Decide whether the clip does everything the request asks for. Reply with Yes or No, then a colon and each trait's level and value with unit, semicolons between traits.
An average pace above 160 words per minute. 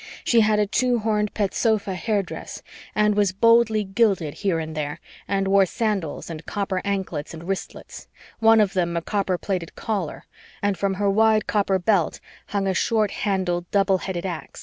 Yes: average, 175 wpm